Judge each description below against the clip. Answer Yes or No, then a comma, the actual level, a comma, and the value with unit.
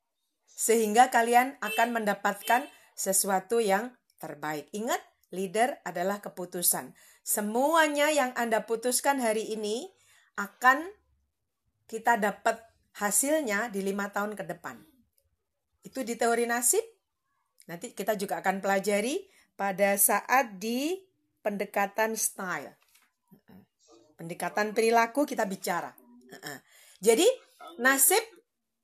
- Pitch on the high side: Yes, high, 220 Hz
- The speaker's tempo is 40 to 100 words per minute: Yes, average, 95 wpm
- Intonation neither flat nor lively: Yes, average, 4.1 semitones